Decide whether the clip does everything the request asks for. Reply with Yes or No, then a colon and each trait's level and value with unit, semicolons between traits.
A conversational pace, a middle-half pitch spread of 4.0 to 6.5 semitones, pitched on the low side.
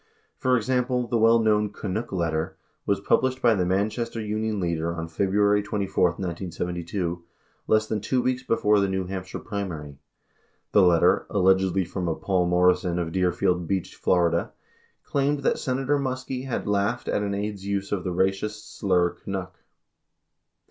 No: average, 160 wpm; average, 3.5 semitones; low, 100 Hz